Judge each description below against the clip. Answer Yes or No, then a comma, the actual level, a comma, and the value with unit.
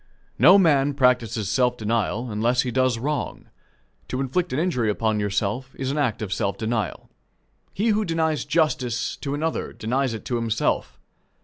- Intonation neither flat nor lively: Yes, average, 4.5 semitones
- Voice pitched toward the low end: Yes, low, 125 Hz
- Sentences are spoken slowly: No, average, 165 wpm